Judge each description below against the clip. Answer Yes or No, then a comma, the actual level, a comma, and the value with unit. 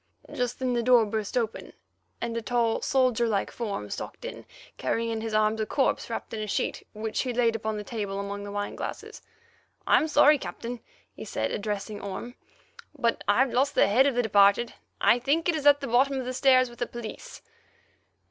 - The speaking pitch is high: Yes, high, 235 Hz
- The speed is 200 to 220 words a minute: Yes, fast, 205 wpm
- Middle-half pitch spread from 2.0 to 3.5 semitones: Yes, average, 2.9 semitones